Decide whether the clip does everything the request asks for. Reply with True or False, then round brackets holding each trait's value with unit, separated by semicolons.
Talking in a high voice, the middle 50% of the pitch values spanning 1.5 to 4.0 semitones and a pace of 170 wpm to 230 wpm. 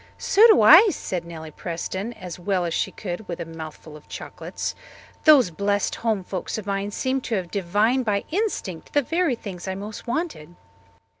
False (200 Hz; 5.5 semitones; 180 wpm)